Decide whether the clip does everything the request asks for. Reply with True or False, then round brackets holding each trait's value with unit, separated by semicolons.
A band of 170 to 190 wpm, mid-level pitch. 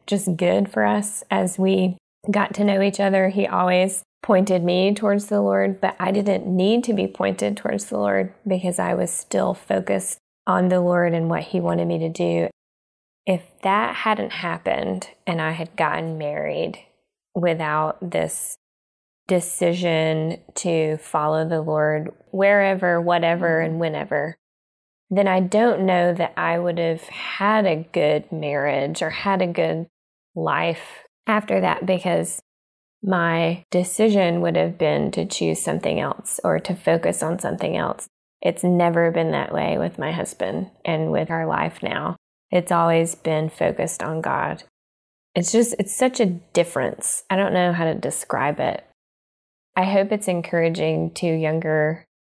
False (155 wpm; 170 Hz)